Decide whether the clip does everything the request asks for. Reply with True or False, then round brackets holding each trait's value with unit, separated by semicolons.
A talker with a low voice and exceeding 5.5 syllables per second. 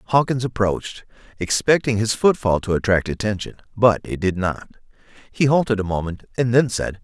False (110 Hz; 5.2 syllables/s)